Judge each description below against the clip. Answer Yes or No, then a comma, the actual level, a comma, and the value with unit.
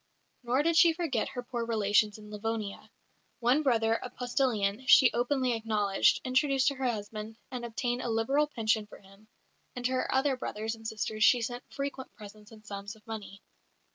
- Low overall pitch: No, high, 230 Hz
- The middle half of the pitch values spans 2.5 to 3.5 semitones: Yes, average, 3.2 semitones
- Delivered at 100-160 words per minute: No, average, 180 wpm